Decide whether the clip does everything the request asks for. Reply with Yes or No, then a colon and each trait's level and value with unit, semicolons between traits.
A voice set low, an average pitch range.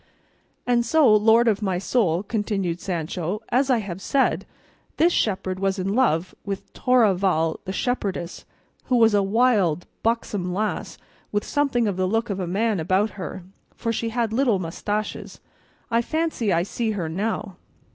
No: high, 205 Hz; average, 3.8 semitones